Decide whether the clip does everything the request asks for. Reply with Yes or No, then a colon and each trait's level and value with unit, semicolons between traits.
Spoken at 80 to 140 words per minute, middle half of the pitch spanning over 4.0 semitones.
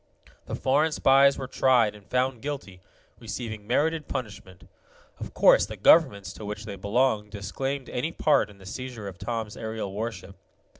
No: average, 160 wpm; average, 4.5 semitones